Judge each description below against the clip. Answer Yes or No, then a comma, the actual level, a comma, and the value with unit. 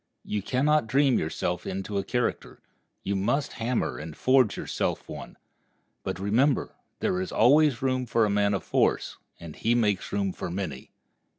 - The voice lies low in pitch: Yes, low, 105 Hz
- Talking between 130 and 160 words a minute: No, average, 170 wpm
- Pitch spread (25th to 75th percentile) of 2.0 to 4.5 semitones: No, average, 5.0 semitones